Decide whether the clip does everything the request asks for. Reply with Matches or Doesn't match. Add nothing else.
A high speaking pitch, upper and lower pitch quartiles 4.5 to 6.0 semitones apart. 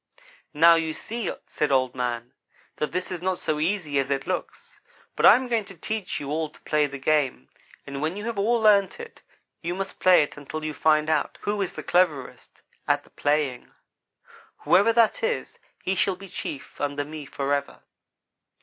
Doesn't match